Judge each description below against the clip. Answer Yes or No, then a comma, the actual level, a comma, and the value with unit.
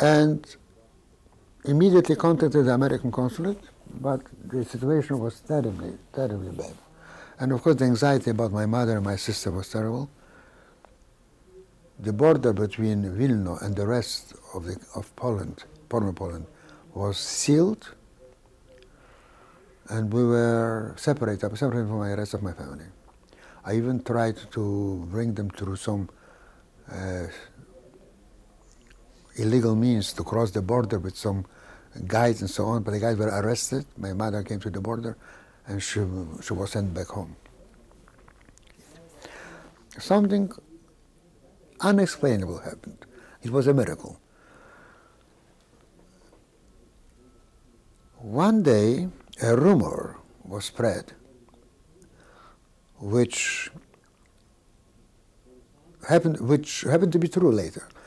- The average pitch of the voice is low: Yes, low, 115 Hz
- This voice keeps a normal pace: No, slow, 115 wpm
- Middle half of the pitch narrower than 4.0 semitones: No, average, 4.7 semitones